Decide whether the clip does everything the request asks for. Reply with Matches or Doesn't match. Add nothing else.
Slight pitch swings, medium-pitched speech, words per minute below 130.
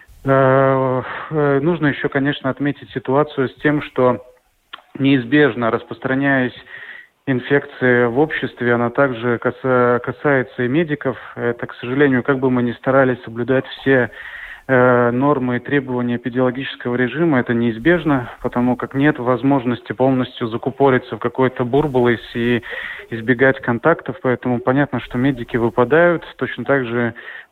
Doesn't match